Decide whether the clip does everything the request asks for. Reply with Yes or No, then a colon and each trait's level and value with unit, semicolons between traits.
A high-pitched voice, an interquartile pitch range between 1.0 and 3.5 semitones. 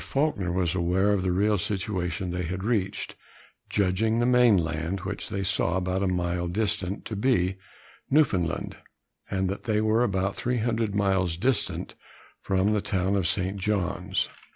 No: very low, 95 Hz; average, 2.8 semitones